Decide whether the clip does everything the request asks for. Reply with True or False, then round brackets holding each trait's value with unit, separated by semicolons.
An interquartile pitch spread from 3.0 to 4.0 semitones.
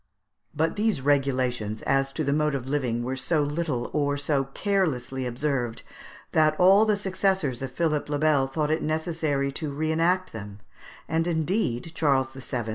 True (3.4 semitones)